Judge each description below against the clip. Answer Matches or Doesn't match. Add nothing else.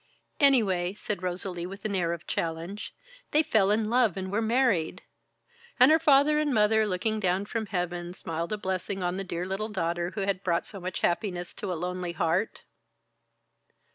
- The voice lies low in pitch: Doesn't match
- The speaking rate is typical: Matches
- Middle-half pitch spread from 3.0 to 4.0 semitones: Matches